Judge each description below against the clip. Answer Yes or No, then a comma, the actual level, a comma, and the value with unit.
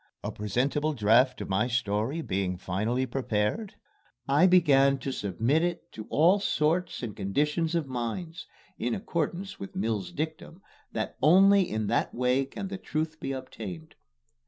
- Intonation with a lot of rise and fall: Yes, wide, 7.1 semitones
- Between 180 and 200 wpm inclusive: No, average, 150 wpm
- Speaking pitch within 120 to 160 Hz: Yes, low, 135 Hz